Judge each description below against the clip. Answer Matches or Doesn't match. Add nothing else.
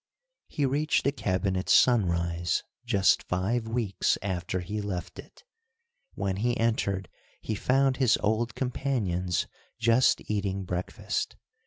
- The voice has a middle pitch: Doesn't match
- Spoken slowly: Matches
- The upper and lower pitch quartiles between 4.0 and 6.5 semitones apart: Matches